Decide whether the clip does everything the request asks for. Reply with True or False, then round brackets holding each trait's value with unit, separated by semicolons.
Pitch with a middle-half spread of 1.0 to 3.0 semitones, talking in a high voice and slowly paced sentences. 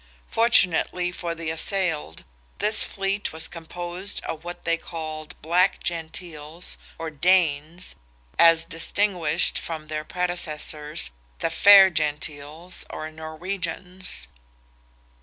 False (2.6 semitones; 165 Hz; 100 wpm)